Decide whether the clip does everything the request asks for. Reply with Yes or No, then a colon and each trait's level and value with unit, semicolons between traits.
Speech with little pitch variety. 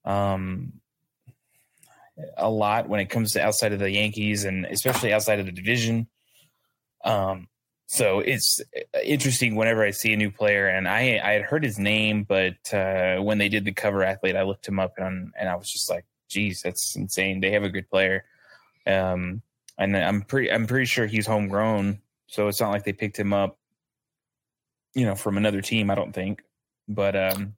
Yes: narrow, 2.3 semitones